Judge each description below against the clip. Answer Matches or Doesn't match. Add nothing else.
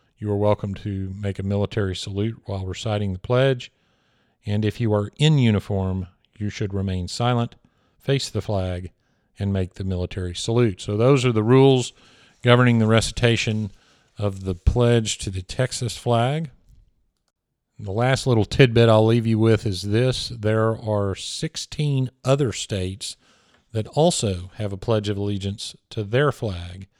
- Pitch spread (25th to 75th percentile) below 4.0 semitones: Matches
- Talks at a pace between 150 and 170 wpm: Matches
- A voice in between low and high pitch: Doesn't match